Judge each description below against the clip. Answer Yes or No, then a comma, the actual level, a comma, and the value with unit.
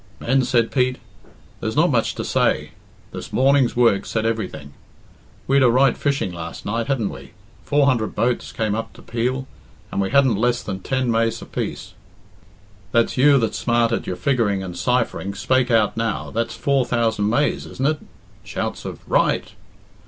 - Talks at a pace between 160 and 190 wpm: Yes, average, 170 wpm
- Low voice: Yes, low, 120 Hz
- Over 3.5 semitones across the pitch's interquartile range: No, average, 3.1 semitones